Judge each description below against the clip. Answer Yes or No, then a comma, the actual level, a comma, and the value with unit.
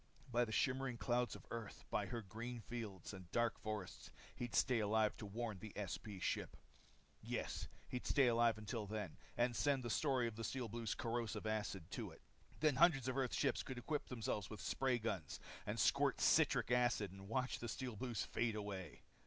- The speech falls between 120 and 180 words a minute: No, average, 190 wpm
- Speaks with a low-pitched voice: Yes, low, 115 Hz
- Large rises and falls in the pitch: No, average, 2.7 semitones